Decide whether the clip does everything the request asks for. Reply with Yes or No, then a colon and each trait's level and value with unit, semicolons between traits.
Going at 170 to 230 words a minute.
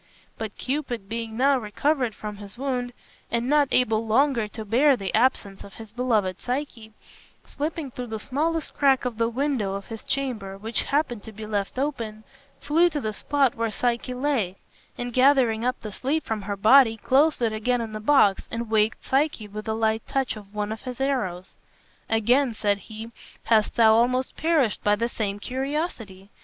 Yes: average, 185 wpm